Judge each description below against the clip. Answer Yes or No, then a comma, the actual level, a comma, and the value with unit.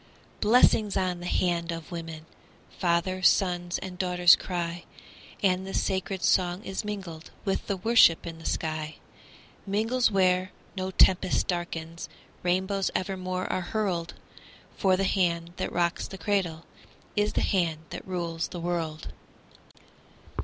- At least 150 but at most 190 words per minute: No, slow, 135 wpm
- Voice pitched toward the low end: No, medium, 180 Hz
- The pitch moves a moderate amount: No, narrow, 2.1 semitones